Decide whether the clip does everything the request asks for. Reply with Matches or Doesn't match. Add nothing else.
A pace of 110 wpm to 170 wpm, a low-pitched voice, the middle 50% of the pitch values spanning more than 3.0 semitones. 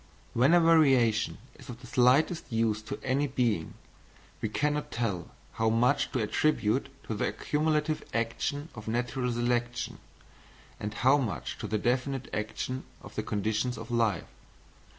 Matches